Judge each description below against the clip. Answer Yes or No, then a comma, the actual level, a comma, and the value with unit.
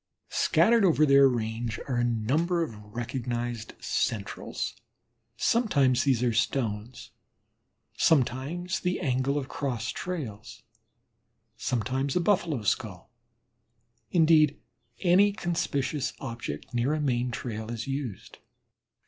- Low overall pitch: Yes, low, 130 Hz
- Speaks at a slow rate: Yes, slow, 105 wpm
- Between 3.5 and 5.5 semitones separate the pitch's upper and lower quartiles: Yes, average, 4.7 semitones